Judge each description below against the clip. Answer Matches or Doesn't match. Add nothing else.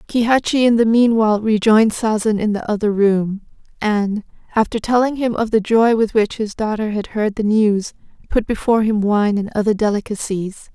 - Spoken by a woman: Matches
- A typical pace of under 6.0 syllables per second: Matches